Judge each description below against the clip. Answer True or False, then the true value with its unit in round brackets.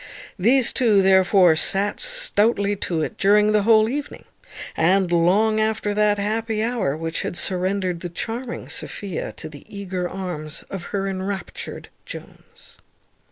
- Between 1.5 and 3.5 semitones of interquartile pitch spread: True (3.1 semitones)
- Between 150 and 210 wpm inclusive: False (140 wpm)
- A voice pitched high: True (200 Hz)